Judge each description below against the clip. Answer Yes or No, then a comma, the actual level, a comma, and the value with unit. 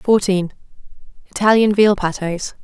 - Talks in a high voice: Yes, high, 195 Hz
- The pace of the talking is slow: Yes, slow, 70 wpm